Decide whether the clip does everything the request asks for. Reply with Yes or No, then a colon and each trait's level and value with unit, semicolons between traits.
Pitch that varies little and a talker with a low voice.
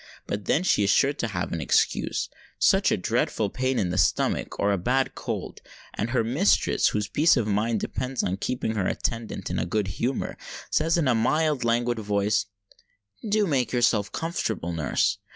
No: average, 4.6 semitones; low, 115 Hz